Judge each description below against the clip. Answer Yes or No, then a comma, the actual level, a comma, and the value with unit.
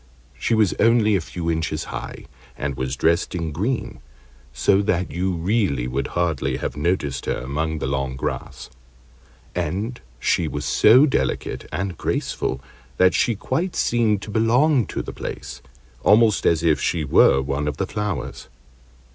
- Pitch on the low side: Yes, very low, 85 Hz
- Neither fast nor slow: Yes, average, 155 wpm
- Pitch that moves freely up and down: Yes, wide, 6.8 semitones